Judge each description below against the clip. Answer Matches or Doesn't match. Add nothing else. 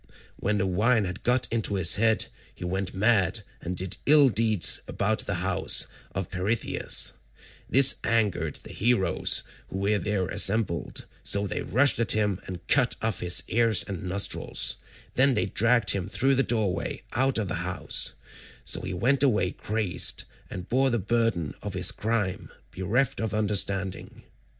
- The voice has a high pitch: Doesn't match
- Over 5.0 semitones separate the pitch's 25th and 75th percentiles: Doesn't match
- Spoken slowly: Doesn't match